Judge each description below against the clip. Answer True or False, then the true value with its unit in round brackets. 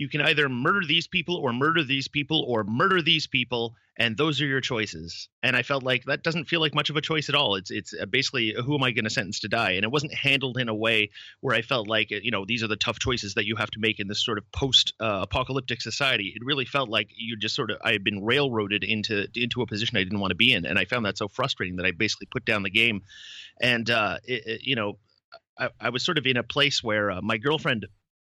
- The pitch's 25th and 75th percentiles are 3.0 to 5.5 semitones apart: True (4.4 semitones)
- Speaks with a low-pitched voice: True (120 Hz)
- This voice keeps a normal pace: False (270 wpm)